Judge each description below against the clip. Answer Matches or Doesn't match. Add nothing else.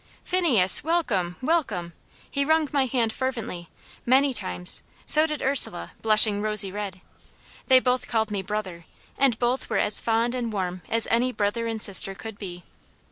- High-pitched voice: Matches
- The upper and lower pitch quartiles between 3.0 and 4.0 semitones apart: Doesn't match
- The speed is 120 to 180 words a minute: Matches